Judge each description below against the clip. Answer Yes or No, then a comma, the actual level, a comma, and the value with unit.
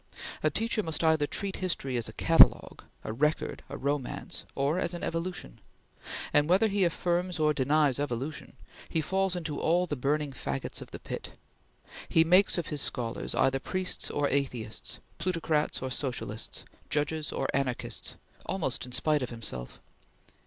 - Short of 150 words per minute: No, average, 160 wpm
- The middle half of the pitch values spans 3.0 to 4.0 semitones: No, average, 4.5 semitones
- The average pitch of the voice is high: No, medium, 150 Hz